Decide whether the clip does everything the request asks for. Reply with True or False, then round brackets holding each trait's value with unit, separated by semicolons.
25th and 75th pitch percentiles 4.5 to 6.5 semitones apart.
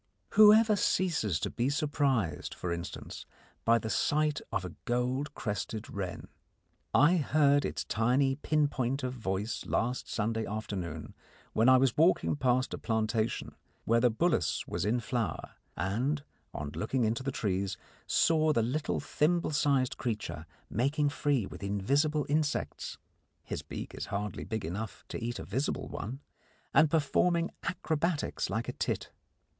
True (5.2 semitones)